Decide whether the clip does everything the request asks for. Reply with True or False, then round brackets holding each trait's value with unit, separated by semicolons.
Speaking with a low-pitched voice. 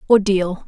False (195 Hz)